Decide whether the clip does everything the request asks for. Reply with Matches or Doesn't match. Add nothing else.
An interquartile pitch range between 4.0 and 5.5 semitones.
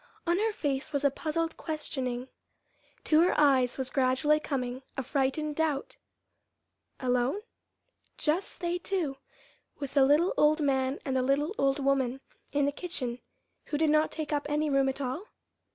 Doesn't match